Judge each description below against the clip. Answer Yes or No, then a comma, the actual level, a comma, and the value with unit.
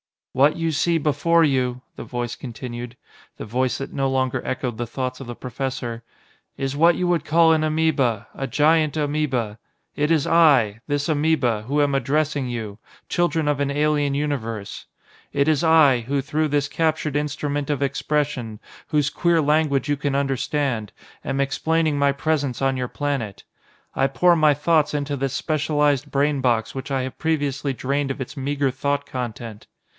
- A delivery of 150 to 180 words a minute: Yes, average, 170 wpm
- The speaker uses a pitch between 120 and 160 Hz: Yes, medium, 140 Hz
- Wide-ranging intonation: No, average, 2.8 semitones